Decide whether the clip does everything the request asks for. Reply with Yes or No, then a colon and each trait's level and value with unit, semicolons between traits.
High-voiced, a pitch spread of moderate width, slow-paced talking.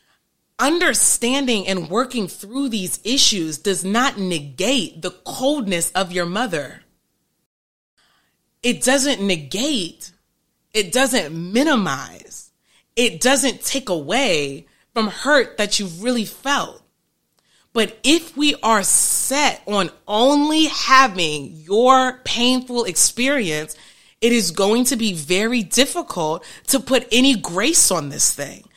No: high, 235 Hz; wide, 5.8 semitones; slow, 115 wpm